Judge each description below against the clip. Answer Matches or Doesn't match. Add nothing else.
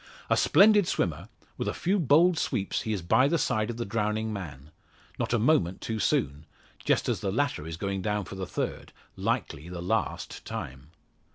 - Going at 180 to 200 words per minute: Matches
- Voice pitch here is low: Matches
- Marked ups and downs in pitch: Matches